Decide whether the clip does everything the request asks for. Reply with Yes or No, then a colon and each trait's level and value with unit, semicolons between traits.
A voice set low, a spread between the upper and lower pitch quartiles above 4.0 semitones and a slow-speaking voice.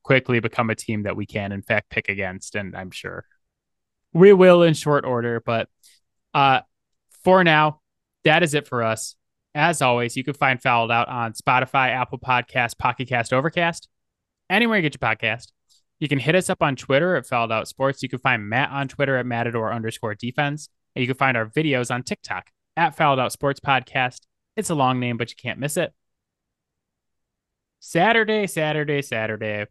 No: low, 125 Hz; average, 4.6 semitones; average, 185 wpm